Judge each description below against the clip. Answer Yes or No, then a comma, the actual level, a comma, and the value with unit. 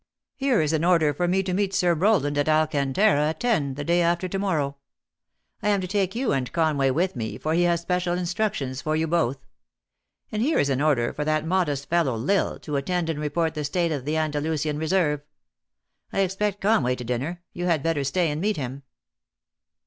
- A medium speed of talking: No, fast, 215 wpm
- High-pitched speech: No, medium, 160 Hz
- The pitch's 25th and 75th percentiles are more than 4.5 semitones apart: No, average, 4.0 semitones